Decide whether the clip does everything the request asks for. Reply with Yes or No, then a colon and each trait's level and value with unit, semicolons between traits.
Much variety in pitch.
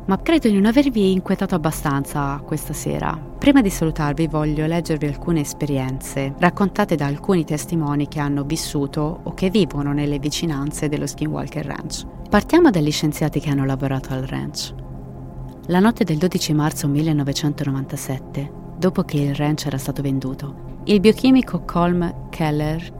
No: average, 3.7 semitones